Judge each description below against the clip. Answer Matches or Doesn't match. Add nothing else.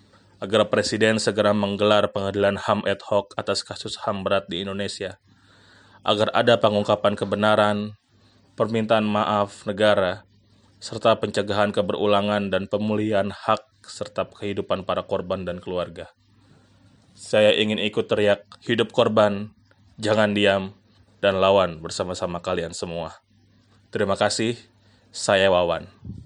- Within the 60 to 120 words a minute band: Matches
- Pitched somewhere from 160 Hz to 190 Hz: Doesn't match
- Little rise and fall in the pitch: Matches